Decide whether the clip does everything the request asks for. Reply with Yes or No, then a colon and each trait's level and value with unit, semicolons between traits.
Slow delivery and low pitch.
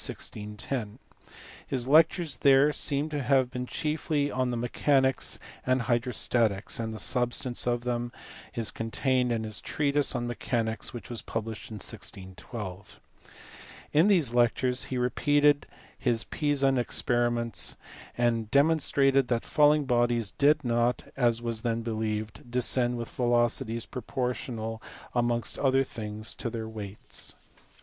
Yes: slow, 125 wpm; low, 120 Hz